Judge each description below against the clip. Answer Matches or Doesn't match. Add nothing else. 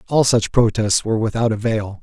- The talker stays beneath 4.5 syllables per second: Doesn't match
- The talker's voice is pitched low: Matches